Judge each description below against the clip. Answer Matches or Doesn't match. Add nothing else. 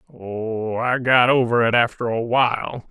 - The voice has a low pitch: Matches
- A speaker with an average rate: Matches